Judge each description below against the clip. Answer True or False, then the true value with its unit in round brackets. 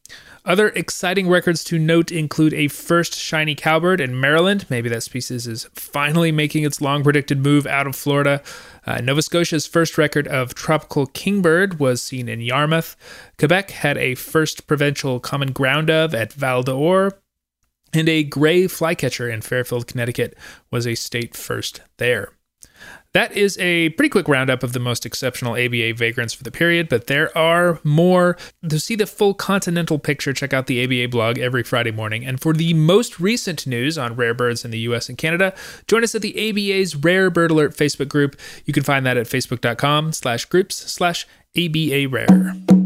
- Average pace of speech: True (175 wpm)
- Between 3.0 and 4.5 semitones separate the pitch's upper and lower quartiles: False (5.1 semitones)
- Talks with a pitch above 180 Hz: False (150 Hz)